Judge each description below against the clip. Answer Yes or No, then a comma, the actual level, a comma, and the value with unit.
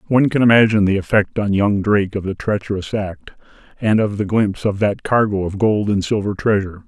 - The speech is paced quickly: Yes, fast, 210 wpm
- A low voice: Yes, low, 105 Hz